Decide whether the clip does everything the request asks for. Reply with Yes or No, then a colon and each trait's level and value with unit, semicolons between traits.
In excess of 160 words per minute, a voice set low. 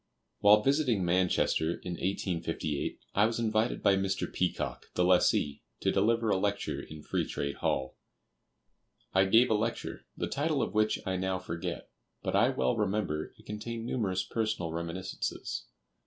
No: average, 155 wpm; very low, 95 Hz